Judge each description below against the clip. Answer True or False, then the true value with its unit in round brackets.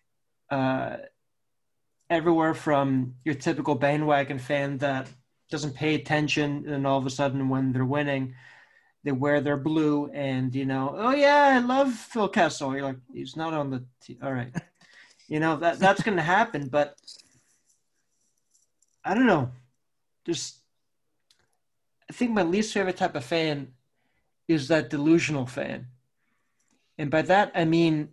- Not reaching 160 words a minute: True (150 wpm)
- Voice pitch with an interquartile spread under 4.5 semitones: True (3.8 semitones)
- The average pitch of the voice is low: False (145 Hz)